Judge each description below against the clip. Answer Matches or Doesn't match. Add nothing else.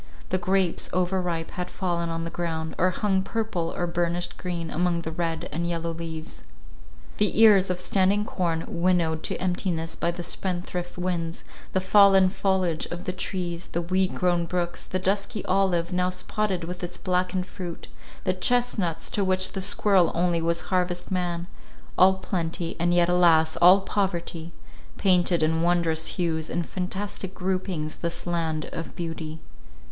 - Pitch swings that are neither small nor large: Doesn't match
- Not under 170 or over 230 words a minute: Doesn't match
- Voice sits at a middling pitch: Matches